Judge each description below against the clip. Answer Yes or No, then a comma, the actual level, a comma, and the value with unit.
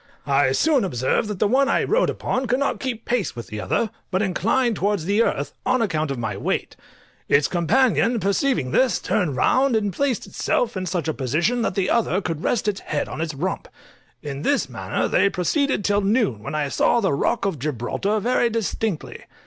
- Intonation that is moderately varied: No, wide, 7.6 semitones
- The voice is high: Yes, high, 200 Hz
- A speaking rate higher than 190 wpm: Yes, average, 200 wpm